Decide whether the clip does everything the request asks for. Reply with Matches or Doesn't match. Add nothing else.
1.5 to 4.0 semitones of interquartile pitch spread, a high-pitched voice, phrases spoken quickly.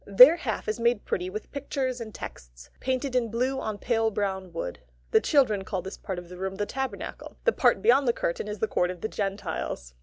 Doesn't match